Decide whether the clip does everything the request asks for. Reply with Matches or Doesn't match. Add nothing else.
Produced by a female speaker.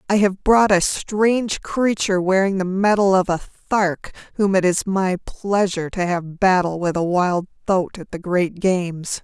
Matches